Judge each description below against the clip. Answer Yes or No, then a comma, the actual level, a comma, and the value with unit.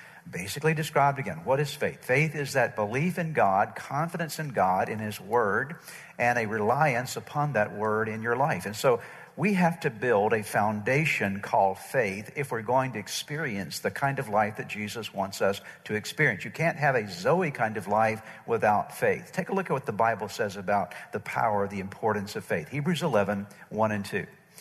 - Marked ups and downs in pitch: Yes, wide, 6.6 semitones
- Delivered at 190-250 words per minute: Yes, average, 200 wpm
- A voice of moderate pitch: No, low, 125 Hz